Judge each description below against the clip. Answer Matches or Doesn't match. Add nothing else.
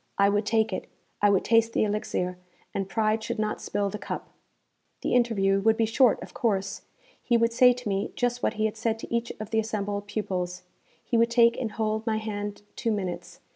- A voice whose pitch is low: Doesn't match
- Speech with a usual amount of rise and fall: Doesn't match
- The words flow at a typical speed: Doesn't match